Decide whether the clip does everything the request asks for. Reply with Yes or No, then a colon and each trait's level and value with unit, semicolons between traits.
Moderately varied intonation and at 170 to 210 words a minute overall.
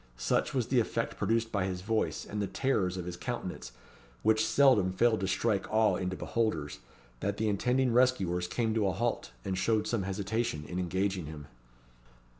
Yes: average, 3.6 semitones; average, 180 wpm